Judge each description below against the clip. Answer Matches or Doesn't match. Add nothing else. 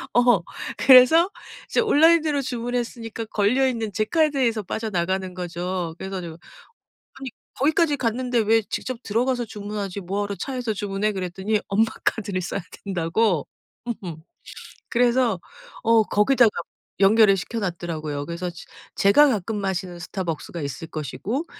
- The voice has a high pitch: Matches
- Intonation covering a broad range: Doesn't match